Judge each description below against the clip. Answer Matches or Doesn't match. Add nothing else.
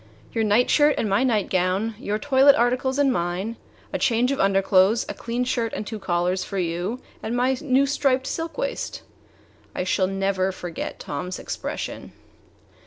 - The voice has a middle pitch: Doesn't match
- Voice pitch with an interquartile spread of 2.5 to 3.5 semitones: Doesn't match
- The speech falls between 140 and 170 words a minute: Matches